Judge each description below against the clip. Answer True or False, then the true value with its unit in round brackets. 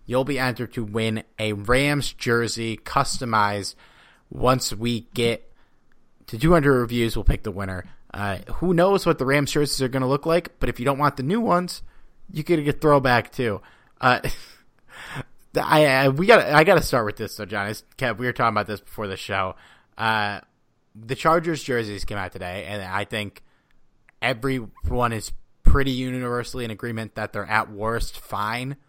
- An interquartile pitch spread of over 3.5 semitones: True (4.4 semitones)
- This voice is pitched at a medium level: False (120 Hz)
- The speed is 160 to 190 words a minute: True (175 wpm)